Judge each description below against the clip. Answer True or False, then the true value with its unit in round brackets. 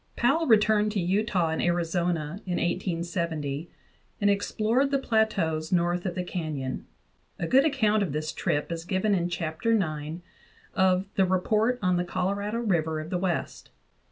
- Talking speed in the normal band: True (155 wpm)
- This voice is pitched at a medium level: True (180 Hz)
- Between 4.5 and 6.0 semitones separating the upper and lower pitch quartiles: False (4.1 semitones)